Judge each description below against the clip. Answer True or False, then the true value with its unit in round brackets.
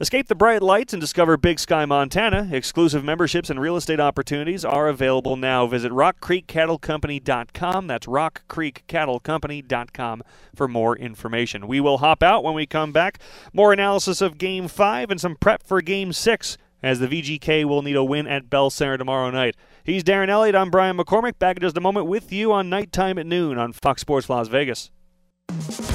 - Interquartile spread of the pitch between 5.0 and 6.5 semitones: True (5.3 semitones)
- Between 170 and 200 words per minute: True (180 wpm)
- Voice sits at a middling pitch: True (160 Hz)